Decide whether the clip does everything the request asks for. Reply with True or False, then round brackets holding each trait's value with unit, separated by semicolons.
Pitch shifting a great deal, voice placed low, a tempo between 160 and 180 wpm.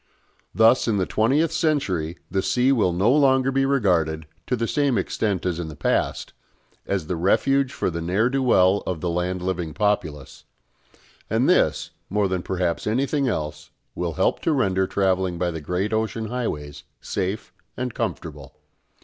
True (6.3 semitones; 95 Hz; 165 wpm)